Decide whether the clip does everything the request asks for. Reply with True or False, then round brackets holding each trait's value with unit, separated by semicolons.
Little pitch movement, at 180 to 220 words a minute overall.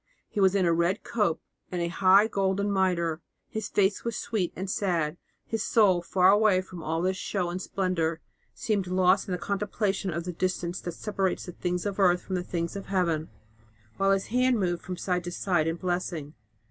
True (2.2 semitones; 200 wpm)